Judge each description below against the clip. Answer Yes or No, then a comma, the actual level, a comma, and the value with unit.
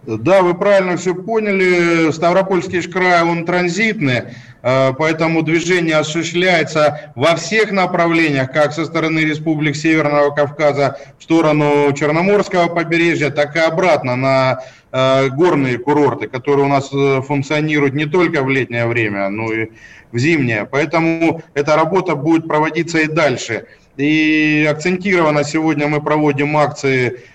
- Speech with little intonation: No, average, 3.3 semitones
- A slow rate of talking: No, average, 125 wpm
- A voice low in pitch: No, medium, 155 Hz